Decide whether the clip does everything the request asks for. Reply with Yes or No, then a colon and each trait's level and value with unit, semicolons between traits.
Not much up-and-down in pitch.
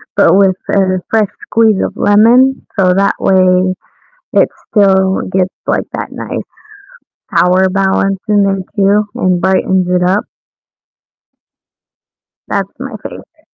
Yes: narrow, 1.7 semitones